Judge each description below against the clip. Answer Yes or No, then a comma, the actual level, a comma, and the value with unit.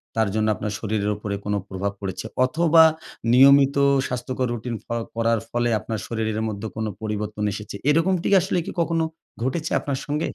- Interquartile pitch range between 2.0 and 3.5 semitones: No, average, 4.8 semitones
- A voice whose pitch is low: Yes, low, 115 Hz